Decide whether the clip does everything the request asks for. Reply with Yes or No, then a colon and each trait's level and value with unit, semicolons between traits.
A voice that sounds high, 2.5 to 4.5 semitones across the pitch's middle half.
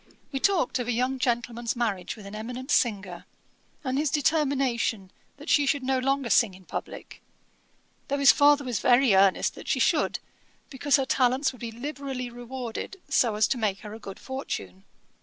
Yes: very high, 250 Hz; average, 3.7 semitones